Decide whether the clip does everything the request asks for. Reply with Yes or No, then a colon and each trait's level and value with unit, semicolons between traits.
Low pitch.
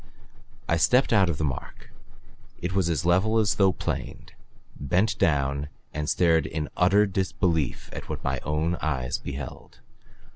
Yes: very low, 80 Hz